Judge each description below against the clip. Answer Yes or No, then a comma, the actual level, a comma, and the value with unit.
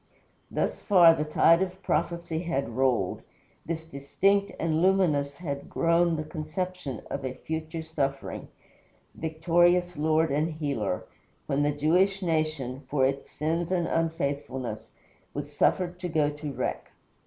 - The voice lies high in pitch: No, medium, 160 Hz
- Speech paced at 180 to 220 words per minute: No, slow, 135 wpm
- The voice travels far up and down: No, average, 3.5 semitones